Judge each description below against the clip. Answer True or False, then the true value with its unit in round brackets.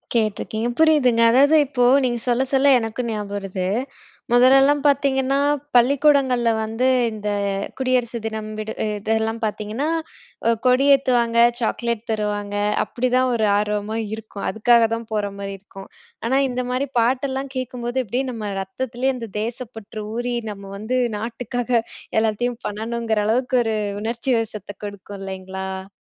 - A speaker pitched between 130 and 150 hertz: False (230 Hz)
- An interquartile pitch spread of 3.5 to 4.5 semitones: False (3.0 semitones)